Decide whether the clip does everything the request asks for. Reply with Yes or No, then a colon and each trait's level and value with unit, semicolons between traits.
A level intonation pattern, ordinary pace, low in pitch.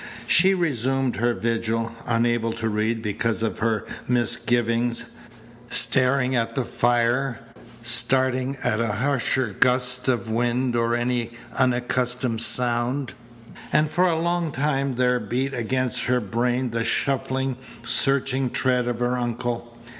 No: narrow, 2.0 semitones; slow, 130 wpm; low, 120 Hz